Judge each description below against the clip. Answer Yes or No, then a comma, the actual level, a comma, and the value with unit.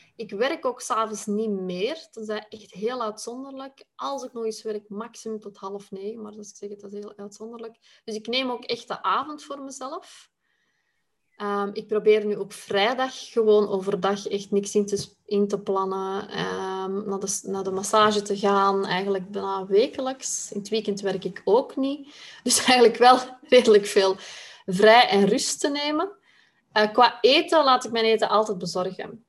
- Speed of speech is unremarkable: Yes, average, 175 wpm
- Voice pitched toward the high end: Yes, high, 215 Hz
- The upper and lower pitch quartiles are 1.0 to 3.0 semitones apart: No, average, 3.5 semitones